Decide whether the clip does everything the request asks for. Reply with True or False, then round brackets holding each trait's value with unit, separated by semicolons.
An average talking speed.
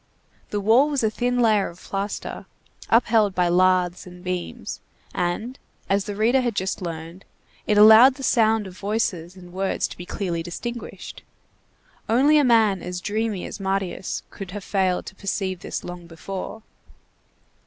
True (160 wpm)